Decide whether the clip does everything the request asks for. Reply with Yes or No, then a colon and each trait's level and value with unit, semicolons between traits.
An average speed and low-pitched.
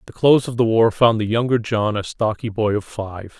No: fast, 245 wpm; low, 110 Hz